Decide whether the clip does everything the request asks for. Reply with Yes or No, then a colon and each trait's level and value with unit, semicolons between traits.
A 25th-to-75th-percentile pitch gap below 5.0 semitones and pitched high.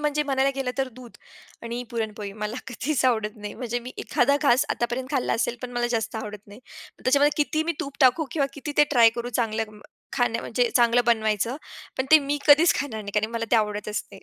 Yes: average, 3.7 semitones; high, 245 Hz